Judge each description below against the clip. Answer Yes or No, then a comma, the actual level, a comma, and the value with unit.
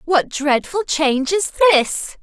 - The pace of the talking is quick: No, slow, 135 wpm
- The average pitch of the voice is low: No, very high, 315 Hz